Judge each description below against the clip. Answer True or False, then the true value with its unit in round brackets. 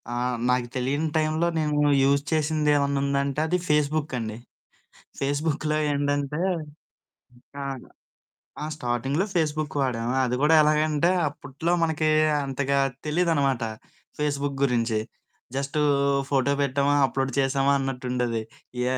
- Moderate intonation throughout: False (2.3 semitones)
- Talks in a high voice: False (140 Hz)